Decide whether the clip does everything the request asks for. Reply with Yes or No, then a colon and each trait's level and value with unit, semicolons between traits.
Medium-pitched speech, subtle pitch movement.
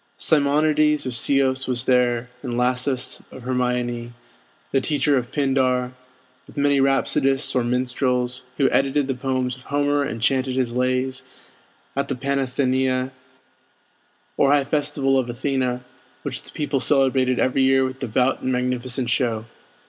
No: low, 130 Hz; narrow, 1.5 semitones